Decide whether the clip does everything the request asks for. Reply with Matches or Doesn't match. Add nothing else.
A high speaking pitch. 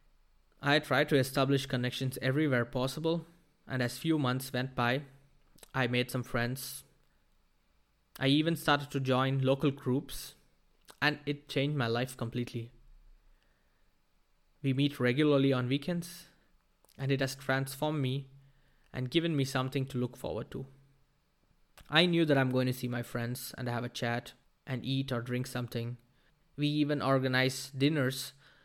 Doesn't match